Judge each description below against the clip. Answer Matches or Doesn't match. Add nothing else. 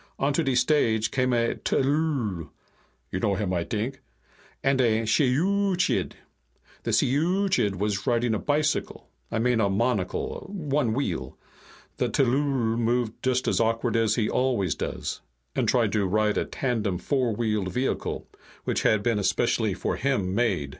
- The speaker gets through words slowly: Doesn't match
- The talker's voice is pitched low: Matches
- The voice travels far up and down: Doesn't match